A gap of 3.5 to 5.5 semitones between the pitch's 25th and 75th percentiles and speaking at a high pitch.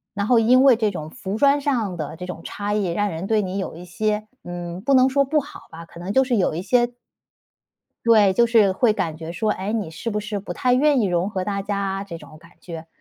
Yes: average, 4.7 semitones; high, 200 Hz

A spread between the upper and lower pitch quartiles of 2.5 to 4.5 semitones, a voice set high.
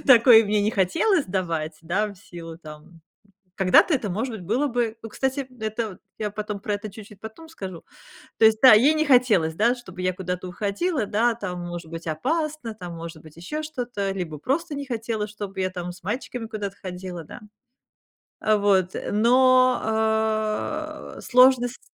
No: average, 5.1 semitones; high, 215 Hz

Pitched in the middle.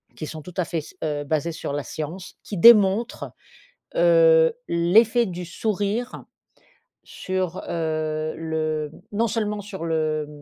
Yes: medium, 175 Hz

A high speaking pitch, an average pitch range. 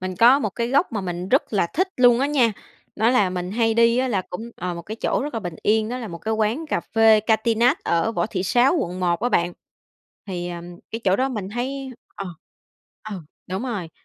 Yes: high, 220 Hz; average, 4.9 semitones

